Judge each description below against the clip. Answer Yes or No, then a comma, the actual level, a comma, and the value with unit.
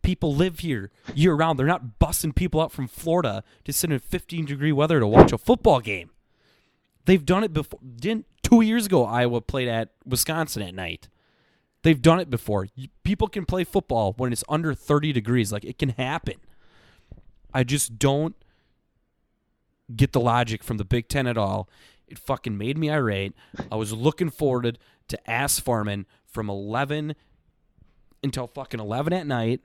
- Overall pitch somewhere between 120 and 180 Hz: Yes, low, 135 Hz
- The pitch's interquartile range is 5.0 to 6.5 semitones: Yes, wide, 5.6 semitones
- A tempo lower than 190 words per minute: Yes, average, 170 wpm